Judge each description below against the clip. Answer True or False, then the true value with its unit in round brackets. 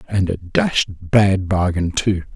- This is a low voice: True (95 Hz)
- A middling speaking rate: True (155 wpm)